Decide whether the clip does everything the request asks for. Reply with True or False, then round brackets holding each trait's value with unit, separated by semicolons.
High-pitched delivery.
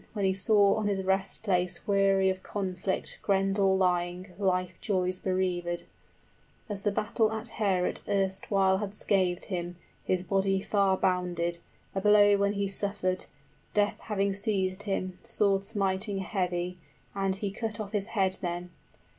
True (195 Hz)